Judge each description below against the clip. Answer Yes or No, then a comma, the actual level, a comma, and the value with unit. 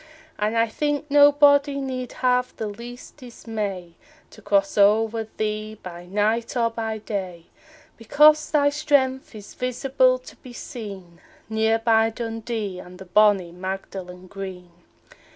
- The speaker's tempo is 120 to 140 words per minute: Yes, slow, 135 wpm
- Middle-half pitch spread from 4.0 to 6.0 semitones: Yes, average, 4.4 semitones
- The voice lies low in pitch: No, high, 225 Hz